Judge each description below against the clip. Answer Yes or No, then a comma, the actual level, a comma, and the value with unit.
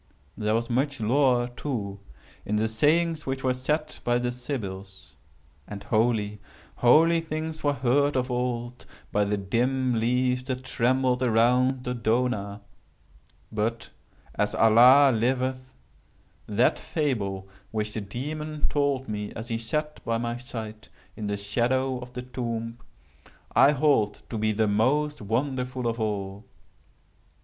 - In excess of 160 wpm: No, slow, 135 wpm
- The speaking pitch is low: Yes, low, 120 Hz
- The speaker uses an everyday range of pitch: Yes, average, 3.2 semitones